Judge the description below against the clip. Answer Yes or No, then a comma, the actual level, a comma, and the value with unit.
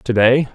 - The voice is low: Yes, low, 125 Hz